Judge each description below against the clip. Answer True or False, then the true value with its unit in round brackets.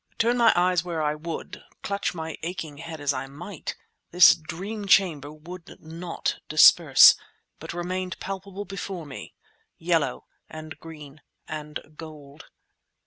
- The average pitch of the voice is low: False (165 Hz)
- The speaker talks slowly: True (130 wpm)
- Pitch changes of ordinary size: True (3.2 semitones)